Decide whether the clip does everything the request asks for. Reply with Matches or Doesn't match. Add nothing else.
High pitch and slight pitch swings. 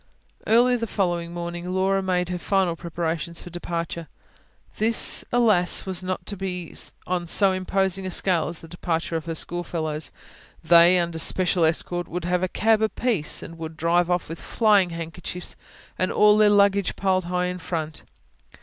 Doesn't match